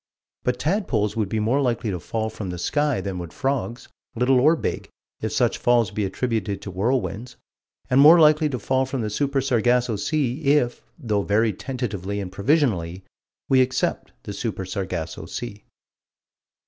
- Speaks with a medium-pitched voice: No, low, 120 Hz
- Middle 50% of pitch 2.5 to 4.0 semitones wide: No, average, 4.8 semitones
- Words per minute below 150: No, average, 165 wpm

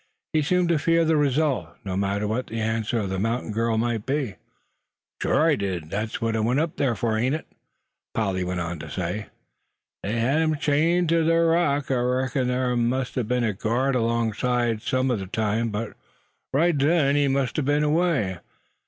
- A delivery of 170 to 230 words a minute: Yes, average, 195 wpm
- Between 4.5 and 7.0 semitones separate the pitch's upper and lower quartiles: Yes, average, 5.0 semitones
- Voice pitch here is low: Yes, low, 125 Hz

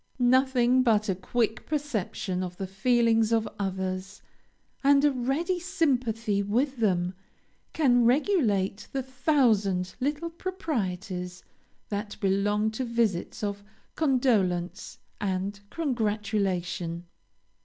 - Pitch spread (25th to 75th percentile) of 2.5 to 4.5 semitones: No, average, 5.3 semitones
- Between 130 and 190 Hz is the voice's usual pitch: No, high, 220 Hz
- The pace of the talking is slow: Yes, slow, 100 wpm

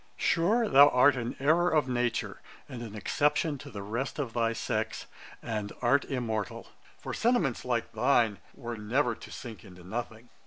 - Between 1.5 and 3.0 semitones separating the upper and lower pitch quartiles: No, average, 4.2 semitones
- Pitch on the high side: No, low, 120 Hz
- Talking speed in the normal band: Yes, average, 165 wpm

